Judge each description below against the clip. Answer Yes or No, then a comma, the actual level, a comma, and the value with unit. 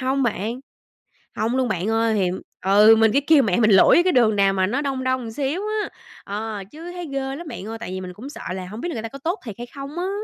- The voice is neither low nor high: No, high, 230 Hz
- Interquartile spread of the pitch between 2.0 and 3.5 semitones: No, average, 4.8 semitones